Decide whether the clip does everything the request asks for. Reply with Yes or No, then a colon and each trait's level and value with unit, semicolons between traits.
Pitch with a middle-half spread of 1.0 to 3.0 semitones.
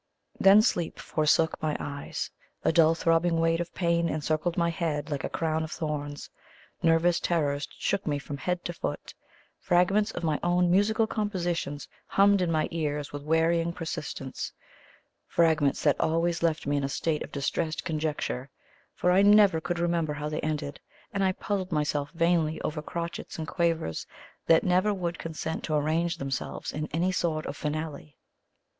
Yes: narrow, 2.4 semitones